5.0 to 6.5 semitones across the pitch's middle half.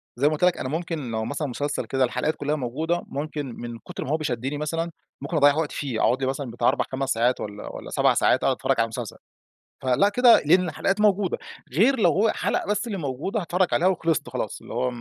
Yes: wide, 5.4 semitones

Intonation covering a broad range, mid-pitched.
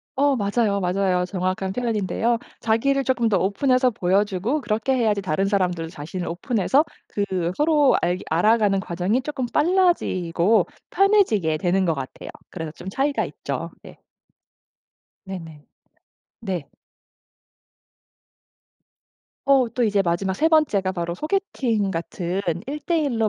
No: wide, 6.2 semitones; high, 205 Hz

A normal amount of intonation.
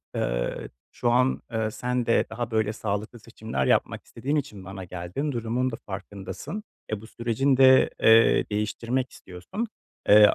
Yes: average, 3.5 semitones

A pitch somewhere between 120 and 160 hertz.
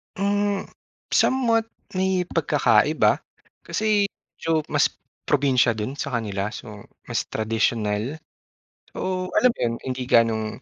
Yes: low, 135 Hz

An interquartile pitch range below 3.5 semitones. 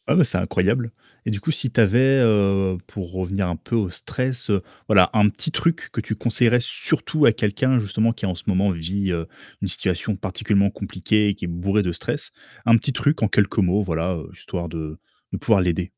No: average, 3.8 semitones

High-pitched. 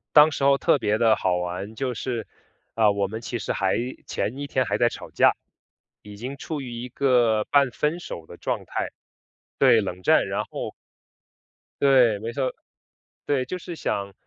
No: low, 120 Hz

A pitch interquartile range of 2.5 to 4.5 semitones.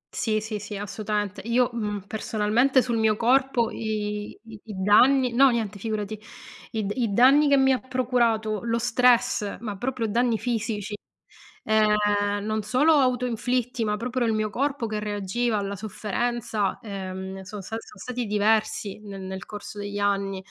Yes: average, 2.8 semitones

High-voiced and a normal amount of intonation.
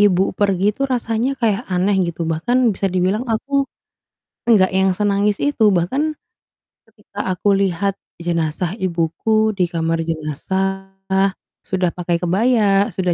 Yes: high, 195 Hz; average, 3.6 semitones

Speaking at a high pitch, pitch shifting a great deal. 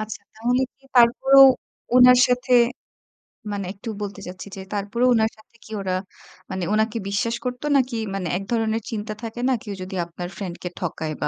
No: high, 220 Hz; average, 3.8 semitones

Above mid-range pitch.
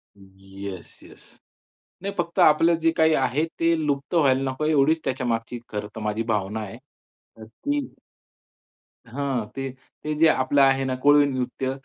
No: low, 135 Hz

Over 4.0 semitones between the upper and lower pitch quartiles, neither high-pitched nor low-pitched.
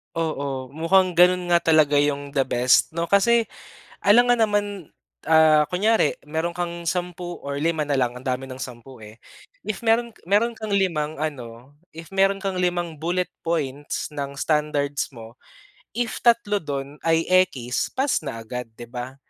Yes: average, 5.0 semitones; medium, 160 Hz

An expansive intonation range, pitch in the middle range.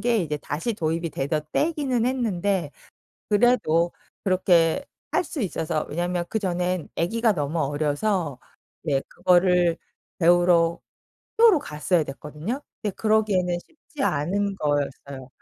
Yes: wide, 5.7 semitones; medium, 175 Hz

